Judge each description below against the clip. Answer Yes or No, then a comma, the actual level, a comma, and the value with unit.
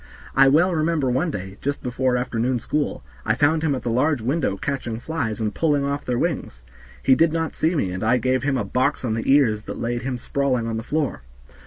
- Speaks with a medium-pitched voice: No, low, 130 Hz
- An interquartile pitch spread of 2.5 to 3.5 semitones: No, average, 4.0 semitones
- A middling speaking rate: No, fast, 225 wpm